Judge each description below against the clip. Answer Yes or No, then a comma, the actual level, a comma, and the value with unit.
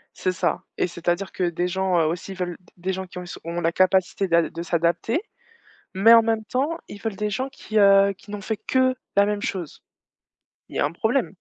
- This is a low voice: No, high, 190 Hz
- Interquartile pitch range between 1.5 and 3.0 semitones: No, average, 3.6 semitones